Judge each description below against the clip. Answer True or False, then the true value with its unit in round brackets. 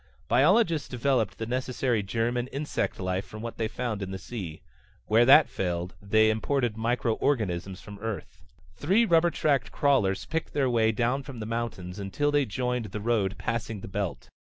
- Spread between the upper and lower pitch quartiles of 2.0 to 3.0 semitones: False (4.6 semitones)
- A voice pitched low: True (115 Hz)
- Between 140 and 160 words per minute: False (175 wpm)